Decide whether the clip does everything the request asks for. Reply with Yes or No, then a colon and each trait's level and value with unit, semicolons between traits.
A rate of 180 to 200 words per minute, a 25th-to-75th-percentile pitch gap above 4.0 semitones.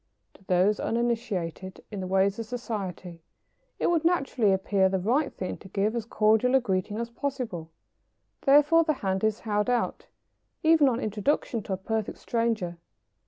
No: average, 165 wpm; average, 4.4 semitones